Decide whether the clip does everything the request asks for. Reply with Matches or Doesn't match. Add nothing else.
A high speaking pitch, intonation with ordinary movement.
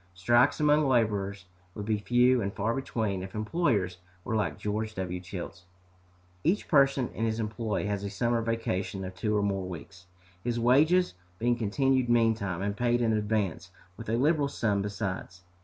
Doesn't match